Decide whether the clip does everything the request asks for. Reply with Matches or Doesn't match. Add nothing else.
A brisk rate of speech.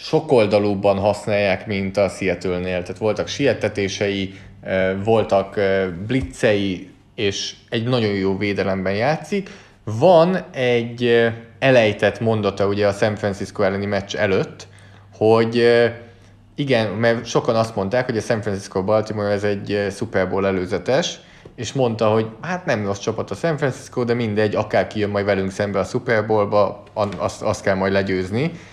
Doesn't match